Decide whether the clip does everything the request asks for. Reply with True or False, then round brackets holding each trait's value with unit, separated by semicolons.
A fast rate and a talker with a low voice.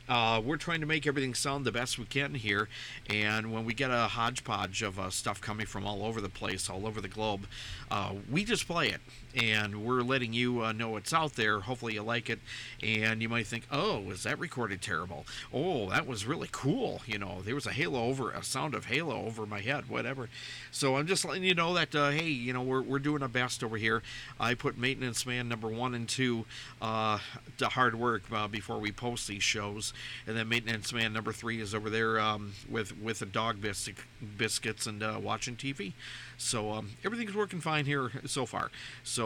True (215 wpm; 115 Hz)